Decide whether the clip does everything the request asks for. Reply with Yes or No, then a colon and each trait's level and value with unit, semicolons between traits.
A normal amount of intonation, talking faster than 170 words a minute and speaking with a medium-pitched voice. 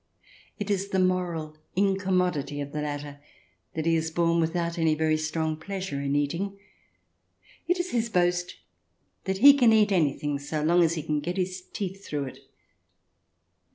No: average, 3.8 semitones; average, 165 wpm; medium, 170 Hz